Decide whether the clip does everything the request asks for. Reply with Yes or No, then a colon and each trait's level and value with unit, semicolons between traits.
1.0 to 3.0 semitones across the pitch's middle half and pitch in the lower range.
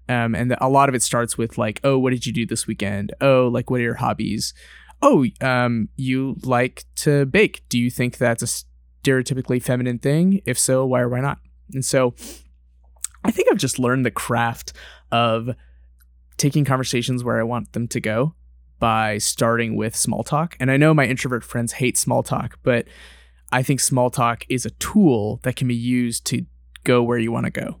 Yes: narrow, 2.6 semitones; low, 120 Hz